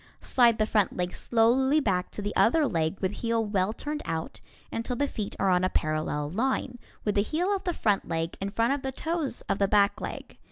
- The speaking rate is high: Yes, fast, 225 wpm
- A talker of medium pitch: No, high, 215 Hz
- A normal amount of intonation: No, wide, 6.0 semitones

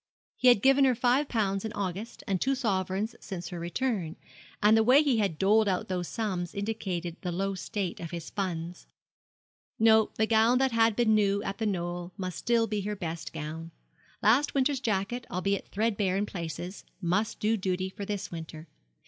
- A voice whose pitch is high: Yes, high, 200 Hz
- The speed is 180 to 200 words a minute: Yes, average, 185 wpm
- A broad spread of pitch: No, average, 3.8 semitones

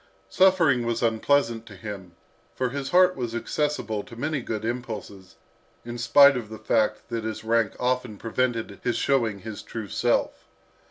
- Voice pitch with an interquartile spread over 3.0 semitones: No, average, 2.7 semitones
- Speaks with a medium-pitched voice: No, low, 115 Hz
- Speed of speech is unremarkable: Yes, average, 160 wpm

